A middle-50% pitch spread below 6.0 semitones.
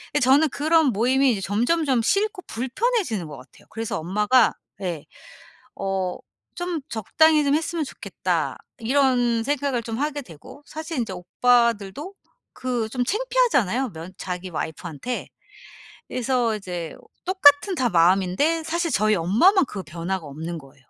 No: wide, 7.8 semitones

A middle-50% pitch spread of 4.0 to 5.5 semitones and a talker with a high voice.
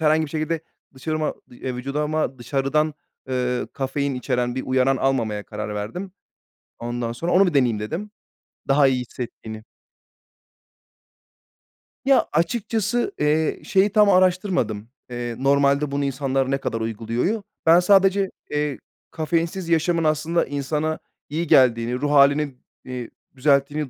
No: average, 4.5 semitones; medium, 140 Hz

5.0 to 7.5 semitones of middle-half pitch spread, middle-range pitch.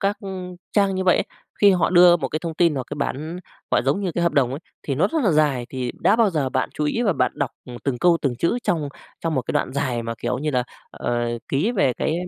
Yes: average, 5.3 semitones; medium, 155 Hz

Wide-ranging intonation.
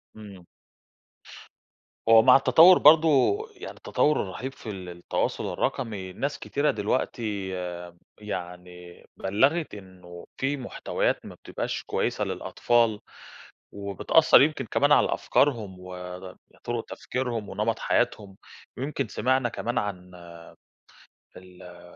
Yes: wide, 6.0 semitones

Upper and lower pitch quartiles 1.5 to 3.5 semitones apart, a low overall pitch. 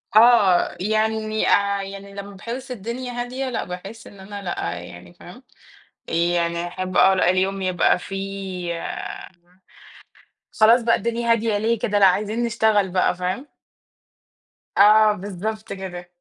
No: average, 3.1 semitones; high, 200 Hz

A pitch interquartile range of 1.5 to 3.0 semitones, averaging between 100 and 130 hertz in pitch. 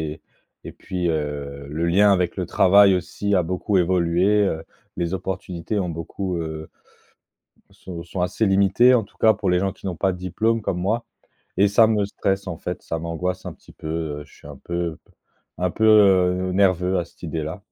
No: average, 2.7 semitones; very low, 90 Hz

